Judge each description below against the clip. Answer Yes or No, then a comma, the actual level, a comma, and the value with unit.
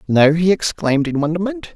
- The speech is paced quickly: No, average, 170 wpm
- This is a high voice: No, medium, 170 Hz